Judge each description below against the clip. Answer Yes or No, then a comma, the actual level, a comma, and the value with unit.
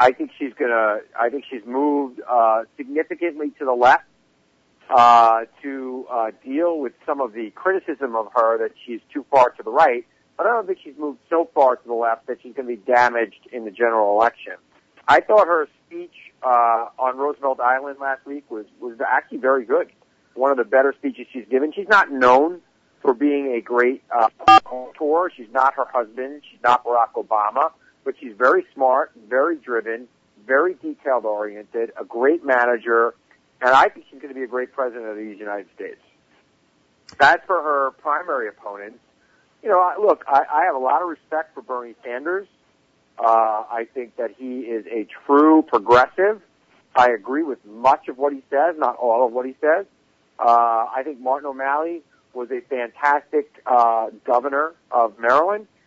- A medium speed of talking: Yes, average, 185 wpm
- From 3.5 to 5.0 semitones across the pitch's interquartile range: Yes, average, 4.7 semitones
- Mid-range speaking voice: No, low, 130 Hz